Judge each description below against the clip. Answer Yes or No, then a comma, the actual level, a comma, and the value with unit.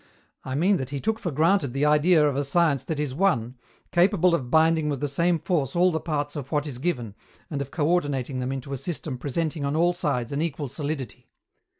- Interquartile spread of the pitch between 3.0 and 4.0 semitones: Yes, average, 3.6 semitones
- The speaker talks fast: Yes, fast, 220 wpm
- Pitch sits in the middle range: Yes, medium, 150 Hz